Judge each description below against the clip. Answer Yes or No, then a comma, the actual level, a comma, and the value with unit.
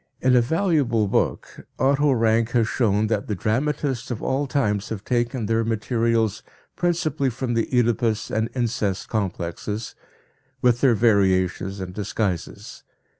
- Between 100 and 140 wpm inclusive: Yes, slow, 135 wpm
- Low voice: Yes, low, 115 Hz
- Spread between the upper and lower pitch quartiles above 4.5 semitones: No, average, 3.3 semitones